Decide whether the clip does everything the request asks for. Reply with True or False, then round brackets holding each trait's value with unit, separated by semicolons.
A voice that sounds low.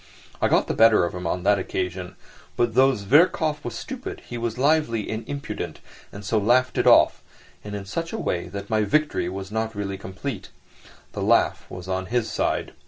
True (110 Hz)